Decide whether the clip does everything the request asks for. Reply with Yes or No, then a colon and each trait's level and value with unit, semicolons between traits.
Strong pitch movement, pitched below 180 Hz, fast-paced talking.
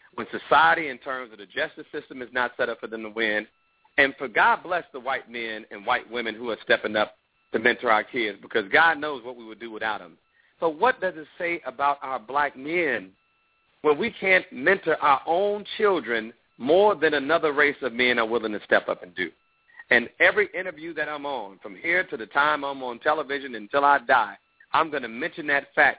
Yes: wide, 5.7 semitones; medium, 140 Hz; fast, 220 wpm